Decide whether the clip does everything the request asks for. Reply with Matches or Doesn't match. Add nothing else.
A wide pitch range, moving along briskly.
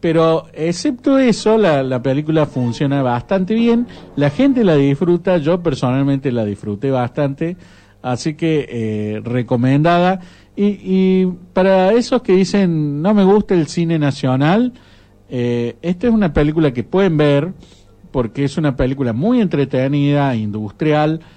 Doesn't match